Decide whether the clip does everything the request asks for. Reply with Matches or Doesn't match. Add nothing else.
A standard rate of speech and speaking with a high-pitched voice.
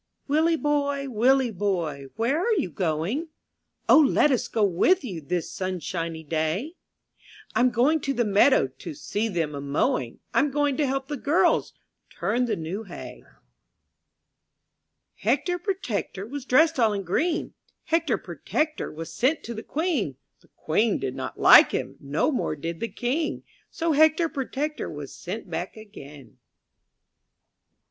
Matches